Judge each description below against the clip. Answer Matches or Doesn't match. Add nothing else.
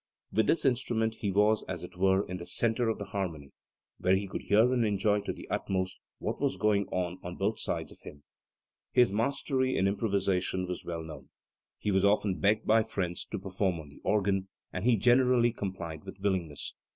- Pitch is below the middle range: Matches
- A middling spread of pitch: Matches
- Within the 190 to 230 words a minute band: Matches